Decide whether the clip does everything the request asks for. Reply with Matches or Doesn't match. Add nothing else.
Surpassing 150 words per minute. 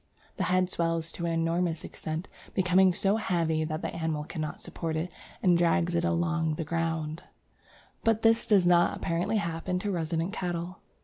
Matches